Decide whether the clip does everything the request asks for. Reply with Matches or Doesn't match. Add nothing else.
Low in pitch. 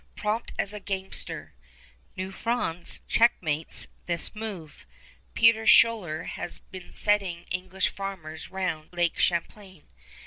Doesn't match